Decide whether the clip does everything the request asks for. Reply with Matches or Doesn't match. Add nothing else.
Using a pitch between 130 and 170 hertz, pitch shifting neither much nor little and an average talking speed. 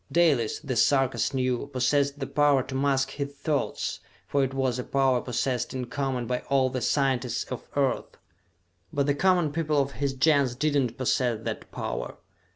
Doesn't match